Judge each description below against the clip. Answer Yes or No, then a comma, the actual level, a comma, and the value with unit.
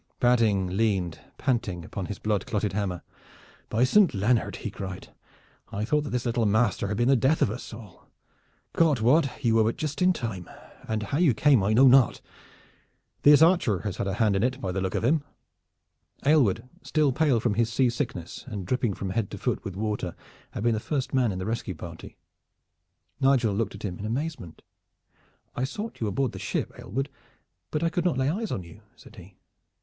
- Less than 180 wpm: No, average, 200 wpm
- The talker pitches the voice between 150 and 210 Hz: No, low, 115 Hz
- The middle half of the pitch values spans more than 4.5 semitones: Yes, average, 5.2 semitones